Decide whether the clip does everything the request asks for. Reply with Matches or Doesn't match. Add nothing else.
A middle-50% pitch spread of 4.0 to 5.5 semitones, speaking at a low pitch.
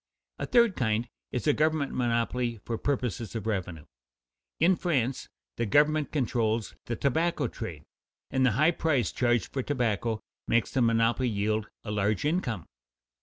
Matches